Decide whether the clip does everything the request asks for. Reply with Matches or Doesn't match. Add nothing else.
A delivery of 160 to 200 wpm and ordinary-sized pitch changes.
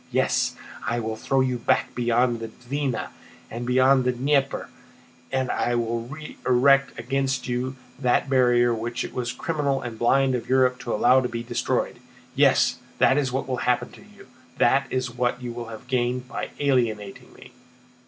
Doesn't match